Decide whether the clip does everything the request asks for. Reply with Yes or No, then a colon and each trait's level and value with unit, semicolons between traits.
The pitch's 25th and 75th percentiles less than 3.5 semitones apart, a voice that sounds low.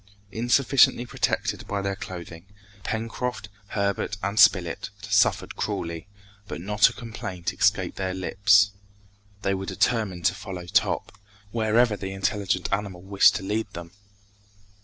Yes: narrow, 2.4 semitones; low, 100 Hz